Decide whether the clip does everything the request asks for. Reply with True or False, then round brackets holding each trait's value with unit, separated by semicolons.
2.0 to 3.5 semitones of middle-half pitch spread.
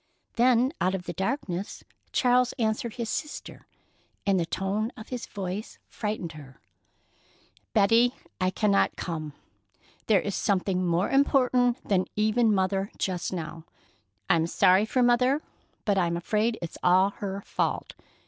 False (4.4 semitones)